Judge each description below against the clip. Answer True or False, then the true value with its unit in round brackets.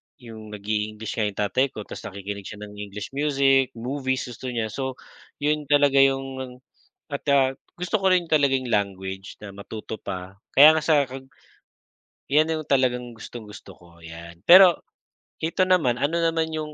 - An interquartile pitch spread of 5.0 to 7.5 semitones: True (5.6 semitones)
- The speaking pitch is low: True (130 Hz)